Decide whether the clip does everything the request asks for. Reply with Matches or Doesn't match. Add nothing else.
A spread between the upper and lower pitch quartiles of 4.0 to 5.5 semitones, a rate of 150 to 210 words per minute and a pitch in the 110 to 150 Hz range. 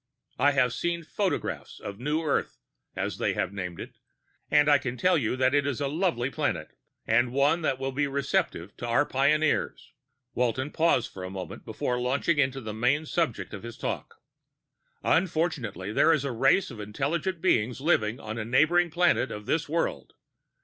Matches